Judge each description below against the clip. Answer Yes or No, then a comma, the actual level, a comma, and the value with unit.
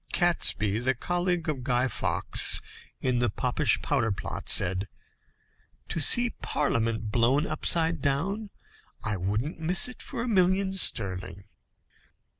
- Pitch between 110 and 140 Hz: Yes, low, 135 Hz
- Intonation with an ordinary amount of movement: No, wide, 7.8 semitones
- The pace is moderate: No, slow, 125 wpm